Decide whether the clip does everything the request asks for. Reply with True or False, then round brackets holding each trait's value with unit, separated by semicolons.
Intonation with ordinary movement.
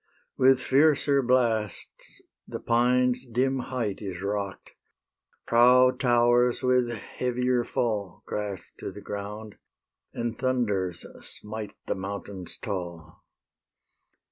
True (3.8 semitones)